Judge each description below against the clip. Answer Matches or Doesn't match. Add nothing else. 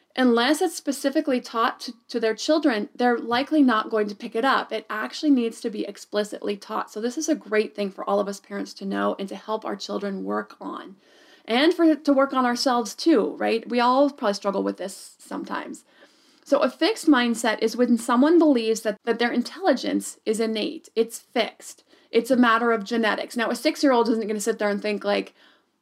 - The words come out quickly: Matches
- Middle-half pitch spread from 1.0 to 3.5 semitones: Doesn't match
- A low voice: Doesn't match